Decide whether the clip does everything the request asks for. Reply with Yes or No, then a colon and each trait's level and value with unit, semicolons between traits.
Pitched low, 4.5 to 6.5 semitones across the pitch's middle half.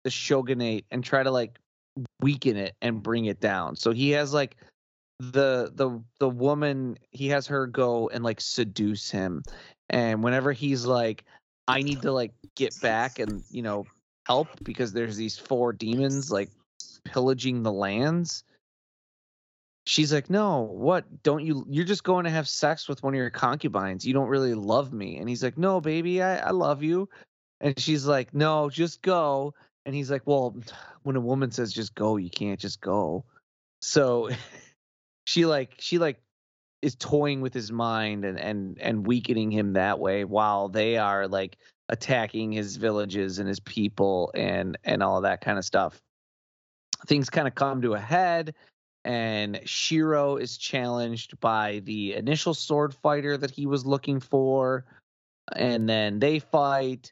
Yes: low, 125 Hz; average, 4.9 semitones